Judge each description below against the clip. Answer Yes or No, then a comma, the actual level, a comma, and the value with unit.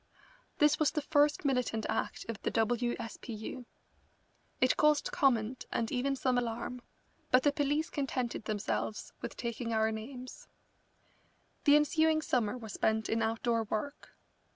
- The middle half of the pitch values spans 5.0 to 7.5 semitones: No, average, 4.1 semitones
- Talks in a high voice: Yes, high, 245 Hz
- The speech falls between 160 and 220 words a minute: No, average, 150 wpm